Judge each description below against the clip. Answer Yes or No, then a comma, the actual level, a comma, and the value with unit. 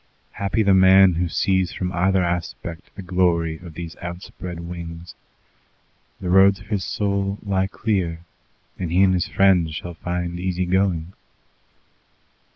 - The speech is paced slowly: No, average, 145 wpm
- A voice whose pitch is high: No, very low, 90 Hz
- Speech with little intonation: Yes, narrow, 1.8 semitones